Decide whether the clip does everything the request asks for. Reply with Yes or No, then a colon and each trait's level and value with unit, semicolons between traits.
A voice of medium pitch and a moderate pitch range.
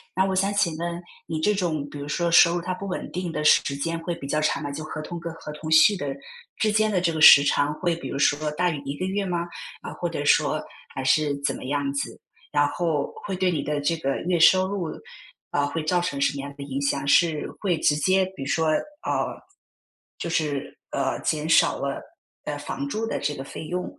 Yes: medium, 160 Hz; average, 3.8 semitones